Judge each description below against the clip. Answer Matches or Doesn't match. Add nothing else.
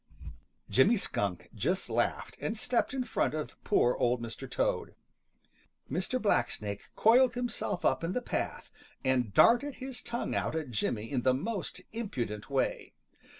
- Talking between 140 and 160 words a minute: Matches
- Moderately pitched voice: Matches